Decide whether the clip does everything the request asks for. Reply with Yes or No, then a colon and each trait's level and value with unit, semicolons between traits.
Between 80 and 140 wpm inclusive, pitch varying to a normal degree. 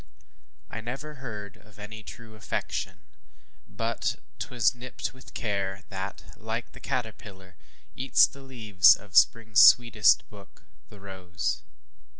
Yes: slow, 135 wpm; average, 3.3 semitones